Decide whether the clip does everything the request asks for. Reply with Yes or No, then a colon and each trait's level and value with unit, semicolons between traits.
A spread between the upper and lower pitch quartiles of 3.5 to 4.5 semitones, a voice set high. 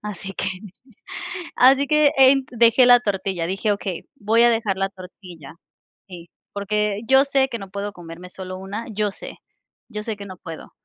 Yes: average, 3.8 semitones; high, 205 Hz